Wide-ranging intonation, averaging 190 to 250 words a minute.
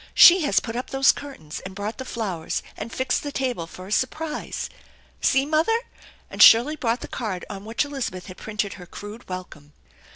Yes: wide, 6.3 semitones; average, 195 wpm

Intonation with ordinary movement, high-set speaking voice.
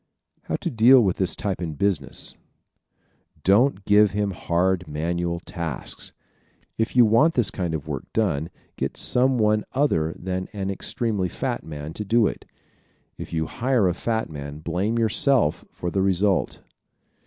No: average, 4.8 semitones; very low, 95 Hz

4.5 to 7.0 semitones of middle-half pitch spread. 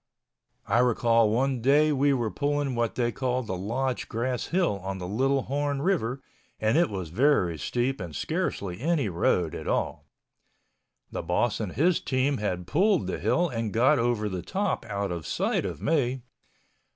Yes: wide, 5.4 semitones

